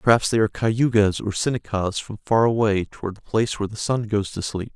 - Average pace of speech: No, fast, 225 wpm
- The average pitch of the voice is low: Yes, low, 105 Hz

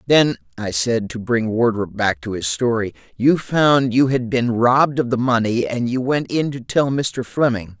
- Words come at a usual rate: No, fast, 210 wpm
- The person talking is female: No, male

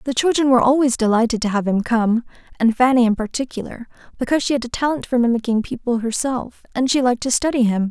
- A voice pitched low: No, high, 245 Hz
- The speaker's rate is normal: No, fast, 215 wpm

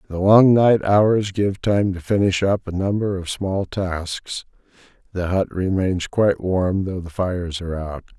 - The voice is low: Yes, very low, 95 Hz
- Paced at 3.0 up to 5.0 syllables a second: Yes, 4.2 syllables/s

